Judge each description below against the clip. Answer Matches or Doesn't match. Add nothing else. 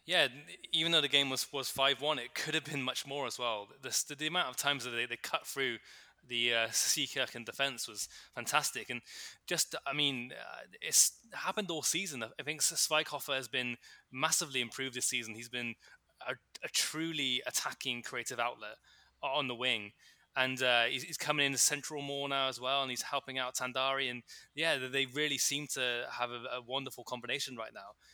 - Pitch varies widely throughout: Doesn't match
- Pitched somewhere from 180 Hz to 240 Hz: Doesn't match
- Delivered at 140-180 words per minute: Doesn't match